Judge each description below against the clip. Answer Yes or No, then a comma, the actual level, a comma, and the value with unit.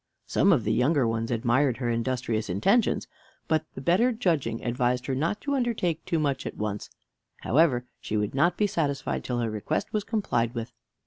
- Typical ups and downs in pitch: No, wide, 6.5 semitones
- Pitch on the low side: Yes, low, 130 Hz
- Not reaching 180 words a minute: No, average, 185 wpm